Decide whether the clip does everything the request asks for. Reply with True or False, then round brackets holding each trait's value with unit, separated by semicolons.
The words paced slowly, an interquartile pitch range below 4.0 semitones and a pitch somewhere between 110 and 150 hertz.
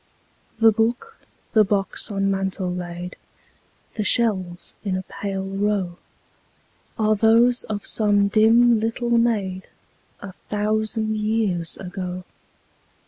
False (110 wpm; 2.8 semitones; 205 Hz)